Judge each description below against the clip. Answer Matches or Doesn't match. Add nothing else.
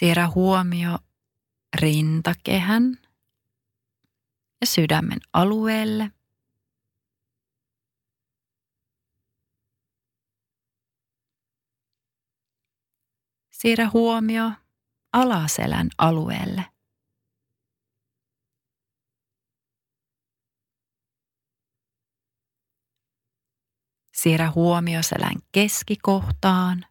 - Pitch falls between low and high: Doesn't match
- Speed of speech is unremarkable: Doesn't match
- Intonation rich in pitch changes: Matches